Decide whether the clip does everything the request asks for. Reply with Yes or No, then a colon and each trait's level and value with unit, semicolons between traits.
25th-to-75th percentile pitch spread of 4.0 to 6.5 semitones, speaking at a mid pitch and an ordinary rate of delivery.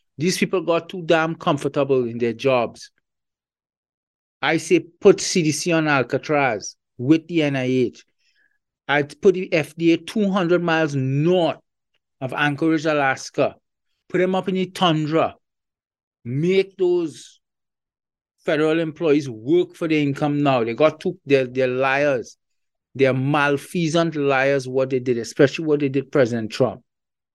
No: average, 4.3 semitones; medium, 155 Hz; slow, 130 wpm